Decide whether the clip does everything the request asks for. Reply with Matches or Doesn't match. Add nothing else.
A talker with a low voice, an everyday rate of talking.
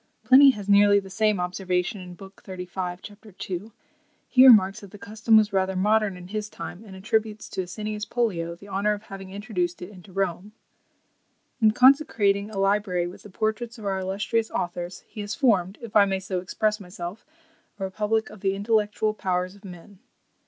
Doesn't match